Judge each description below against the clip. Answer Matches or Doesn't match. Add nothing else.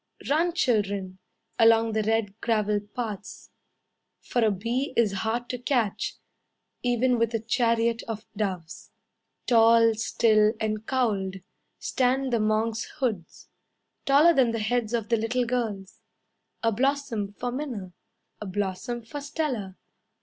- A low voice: Doesn't match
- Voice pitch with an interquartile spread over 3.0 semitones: Doesn't match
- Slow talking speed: Matches